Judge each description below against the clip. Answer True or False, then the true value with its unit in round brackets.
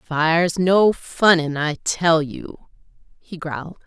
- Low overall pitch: False (165 Hz)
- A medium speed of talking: False (125 wpm)